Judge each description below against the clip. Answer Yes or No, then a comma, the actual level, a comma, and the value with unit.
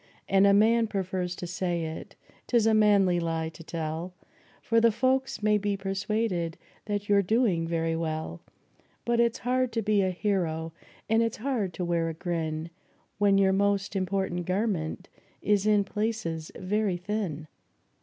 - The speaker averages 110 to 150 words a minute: No, average, 160 wpm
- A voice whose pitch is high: Yes, high, 195 Hz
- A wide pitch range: No, average, 4.0 semitones